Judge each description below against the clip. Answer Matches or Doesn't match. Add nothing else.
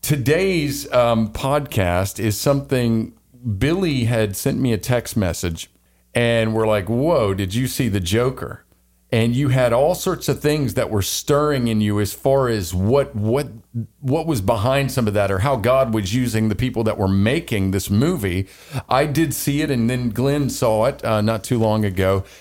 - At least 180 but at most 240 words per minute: Matches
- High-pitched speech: Doesn't match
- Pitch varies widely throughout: Doesn't match